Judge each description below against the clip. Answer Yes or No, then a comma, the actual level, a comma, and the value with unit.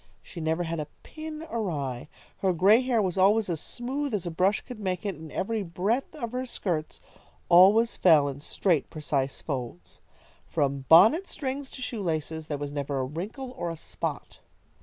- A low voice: No, medium, 180 Hz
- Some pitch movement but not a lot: No, wide, 7.0 semitones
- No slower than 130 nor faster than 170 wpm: No, average, 180 wpm